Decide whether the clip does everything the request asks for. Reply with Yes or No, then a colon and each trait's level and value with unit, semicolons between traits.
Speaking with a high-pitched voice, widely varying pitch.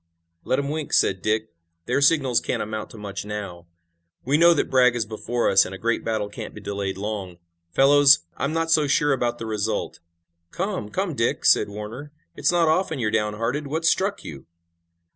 No: low, 120 Hz; wide, 5.8 semitones